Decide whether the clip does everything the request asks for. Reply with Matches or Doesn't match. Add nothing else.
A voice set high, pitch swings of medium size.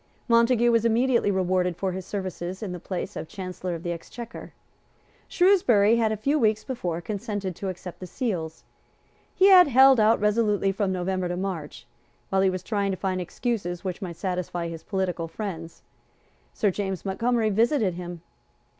Matches